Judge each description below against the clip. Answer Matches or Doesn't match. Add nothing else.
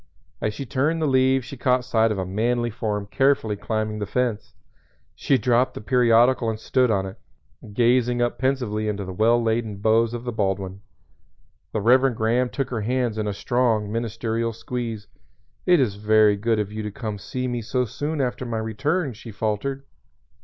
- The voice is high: Doesn't match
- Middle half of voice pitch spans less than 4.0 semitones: Matches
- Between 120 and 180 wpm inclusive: Doesn't match